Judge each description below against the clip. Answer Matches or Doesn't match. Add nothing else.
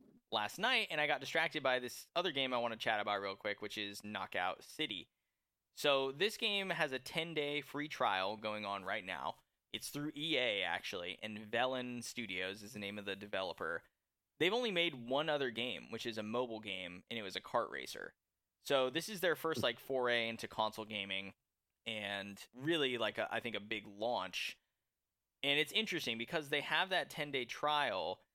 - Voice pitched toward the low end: Matches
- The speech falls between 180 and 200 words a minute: Matches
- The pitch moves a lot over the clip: Matches